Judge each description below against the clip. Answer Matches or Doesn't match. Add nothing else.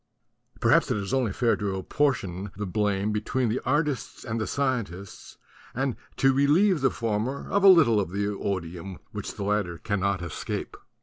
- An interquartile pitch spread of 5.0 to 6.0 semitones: Matches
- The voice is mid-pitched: Doesn't match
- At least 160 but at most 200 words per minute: Matches